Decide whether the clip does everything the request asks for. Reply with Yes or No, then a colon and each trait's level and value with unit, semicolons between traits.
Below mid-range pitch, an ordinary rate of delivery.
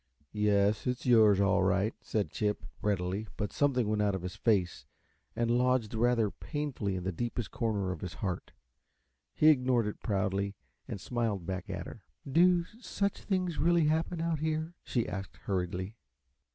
Yes: low, 110 Hz; average, 165 wpm